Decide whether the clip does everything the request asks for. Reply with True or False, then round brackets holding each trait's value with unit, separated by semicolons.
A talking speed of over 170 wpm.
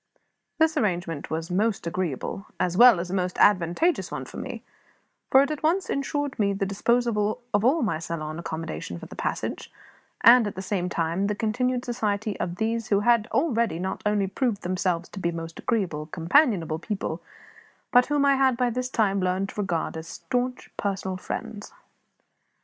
True (180 wpm)